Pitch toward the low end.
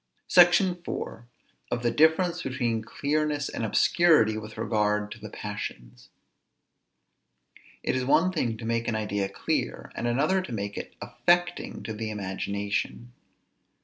Yes: low, 115 Hz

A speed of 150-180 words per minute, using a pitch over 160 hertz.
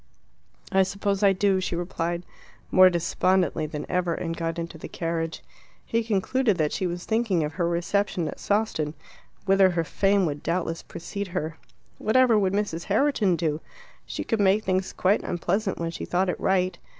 Yes: average, 175 wpm; medium, 185 Hz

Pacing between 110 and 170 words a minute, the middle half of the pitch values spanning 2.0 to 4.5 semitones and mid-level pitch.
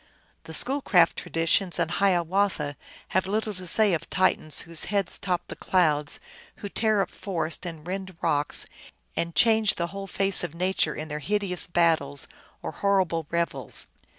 Yes: average, 155 wpm; average, 3.3 semitones; medium, 175 Hz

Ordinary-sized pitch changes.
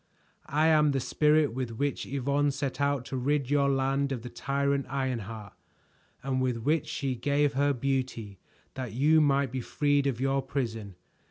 No: narrow, 2.0 semitones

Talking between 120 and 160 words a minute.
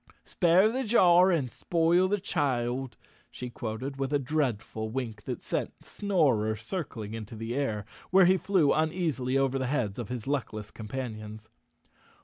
Yes: average, 150 wpm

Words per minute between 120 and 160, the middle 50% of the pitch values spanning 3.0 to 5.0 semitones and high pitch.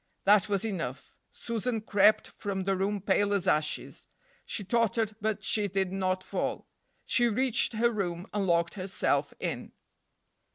No: average, 150 wpm; narrow, 2.6 semitones; high, 200 Hz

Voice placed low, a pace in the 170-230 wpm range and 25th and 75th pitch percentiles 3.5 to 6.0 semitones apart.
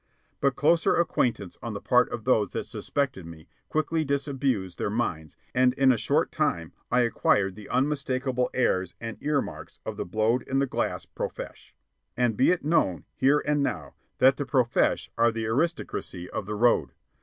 Yes: low, 125 Hz; average, 180 wpm; average, 4.6 semitones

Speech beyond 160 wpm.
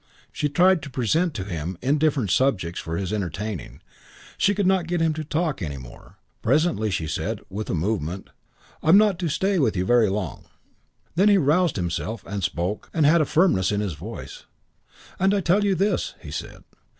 Yes: average, 195 wpm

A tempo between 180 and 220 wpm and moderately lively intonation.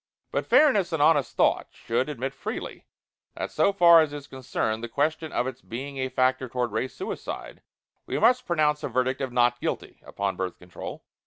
Yes: average, 185 wpm; average, 4.0 semitones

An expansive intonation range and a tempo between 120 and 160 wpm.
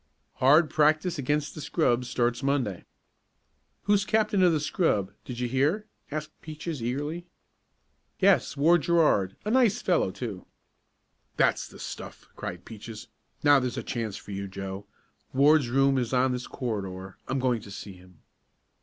Yes: wide, 6.1 semitones; average, 155 wpm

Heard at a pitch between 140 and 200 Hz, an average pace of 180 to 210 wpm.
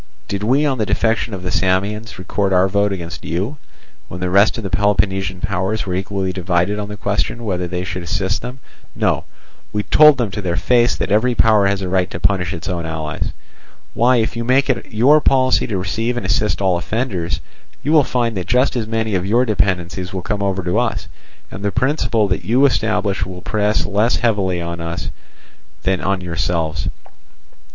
No: low, 100 Hz; average, 200 wpm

